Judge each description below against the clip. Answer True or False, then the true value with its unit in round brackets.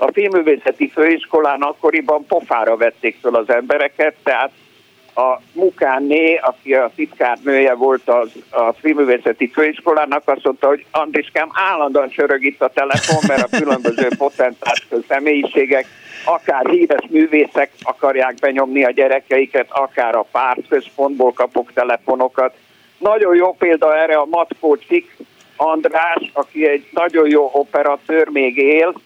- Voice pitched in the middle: True (145 Hz)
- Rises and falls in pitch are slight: False (3.4 semitones)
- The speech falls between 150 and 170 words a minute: False (125 wpm)